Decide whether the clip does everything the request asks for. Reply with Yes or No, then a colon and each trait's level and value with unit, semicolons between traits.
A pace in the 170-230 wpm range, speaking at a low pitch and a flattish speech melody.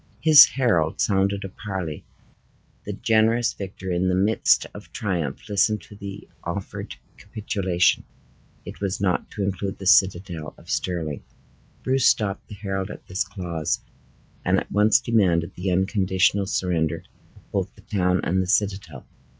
No: average, 145 wpm; very low, 95 Hz; narrow, 2.2 semitones